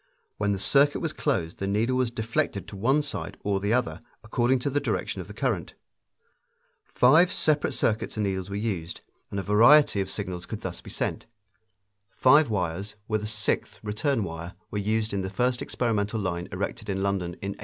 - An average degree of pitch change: Yes, average, 4.2 semitones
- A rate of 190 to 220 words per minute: Yes, average, 195 wpm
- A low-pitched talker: Yes, low, 105 Hz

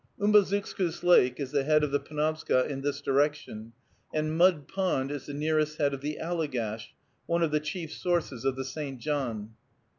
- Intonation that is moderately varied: Yes, average, 3.1 semitones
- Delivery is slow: No, average, 180 wpm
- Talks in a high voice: No, medium, 150 Hz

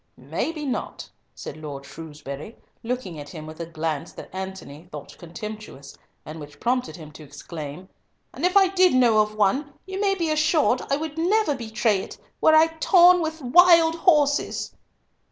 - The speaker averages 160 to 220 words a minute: Yes, average, 170 wpm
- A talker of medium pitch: No, high, 230 Hz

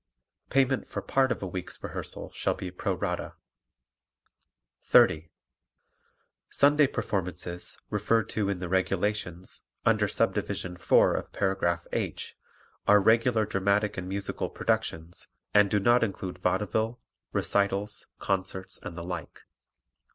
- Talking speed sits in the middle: No, slow, 120 wpm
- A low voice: Yes, low, 100 Hz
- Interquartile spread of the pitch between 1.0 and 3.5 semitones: Yes, average, 2.8 semitones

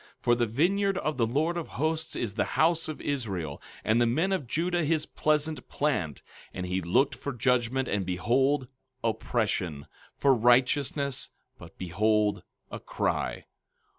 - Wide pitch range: Yes, wide, 6.0 semitones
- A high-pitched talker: No, low, 130 Hz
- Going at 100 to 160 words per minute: Yes, average, 155 wpm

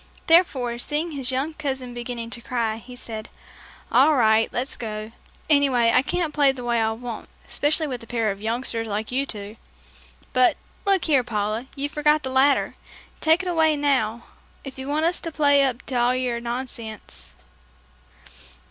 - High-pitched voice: Yes, very high, 255 Hz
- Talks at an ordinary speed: Yes, average, 175 wpm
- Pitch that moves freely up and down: No, average, 3.9 semitones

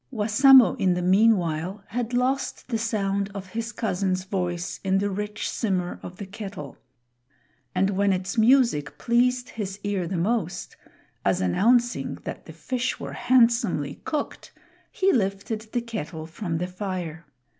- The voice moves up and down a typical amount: Yes, average, 4.2 semitones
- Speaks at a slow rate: No, average, 145 wpm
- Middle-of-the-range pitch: No, high, 200 Hz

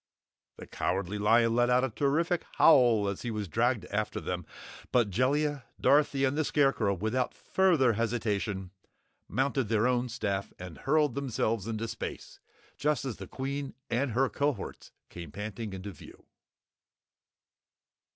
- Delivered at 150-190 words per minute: No, average, 140 wpm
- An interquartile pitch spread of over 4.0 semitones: Yes, average, 4.8 semitones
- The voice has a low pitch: Yes, low, 120 Hz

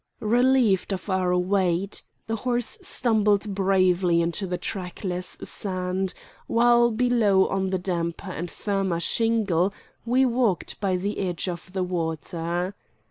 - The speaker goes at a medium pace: No, slow, 130 wpm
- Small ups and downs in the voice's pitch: No, average, 3.3 semitones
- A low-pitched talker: No, high, 190 Hz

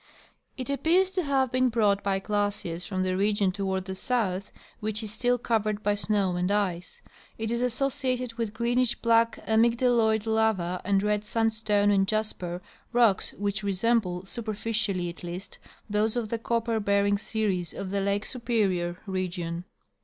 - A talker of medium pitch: No, high, 210 Hz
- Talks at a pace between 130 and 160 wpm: Yes, average, 155 wpm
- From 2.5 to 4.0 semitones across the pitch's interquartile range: Yes, average, 3.1 semitones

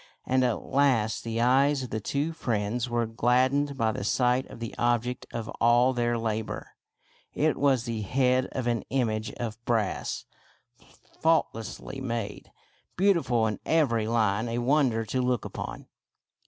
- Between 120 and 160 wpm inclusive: Yes, average, 155 wpm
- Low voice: Yes, low, 120 Hz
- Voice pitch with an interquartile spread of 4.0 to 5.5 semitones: No, narrow, 2.5 semitones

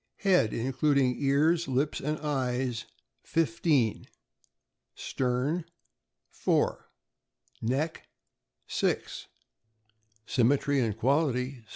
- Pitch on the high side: No, low, 135 Hz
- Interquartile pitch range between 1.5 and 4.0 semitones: Yes, average, 3.4 semitones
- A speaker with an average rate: No, slow, 70 wpm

